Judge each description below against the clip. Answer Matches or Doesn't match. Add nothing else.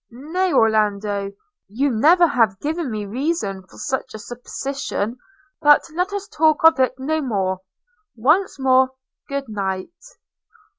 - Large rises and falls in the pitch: Matches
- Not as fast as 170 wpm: Matches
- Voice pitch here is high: Matches